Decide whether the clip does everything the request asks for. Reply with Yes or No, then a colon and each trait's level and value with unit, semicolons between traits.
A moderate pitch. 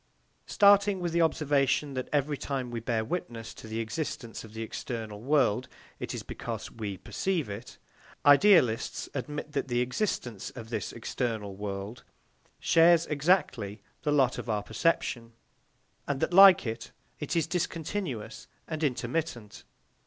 No: low, 130 Hz